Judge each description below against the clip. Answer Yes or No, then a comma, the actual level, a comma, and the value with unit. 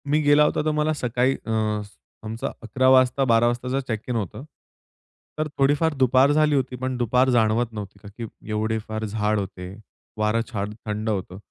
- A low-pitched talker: Yes, low, 120 Hz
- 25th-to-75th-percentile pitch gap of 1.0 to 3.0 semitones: No, average, 3.5 semitones